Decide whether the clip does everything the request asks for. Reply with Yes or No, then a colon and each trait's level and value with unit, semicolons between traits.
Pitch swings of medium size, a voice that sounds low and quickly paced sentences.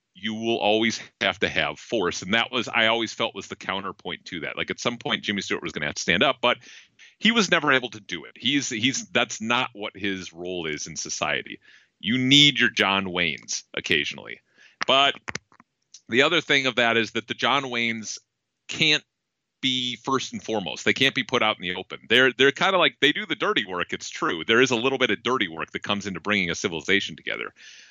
Yes: average, 4.2 semitones; low, 115 Hz; fast, 230 wpm